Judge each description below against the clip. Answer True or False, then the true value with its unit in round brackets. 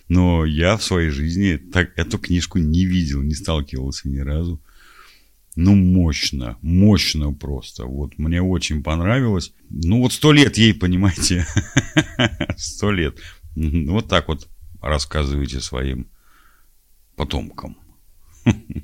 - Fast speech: False (115 wpm)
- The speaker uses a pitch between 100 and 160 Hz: False (85 Hz)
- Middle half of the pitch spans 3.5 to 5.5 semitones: True (4.0 semitones)